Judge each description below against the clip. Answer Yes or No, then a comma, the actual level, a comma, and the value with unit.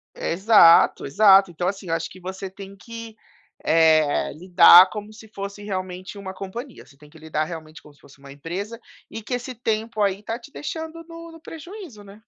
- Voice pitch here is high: Yes, high, 195 Hz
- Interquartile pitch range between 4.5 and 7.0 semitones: Yes, average, 5.0 semitones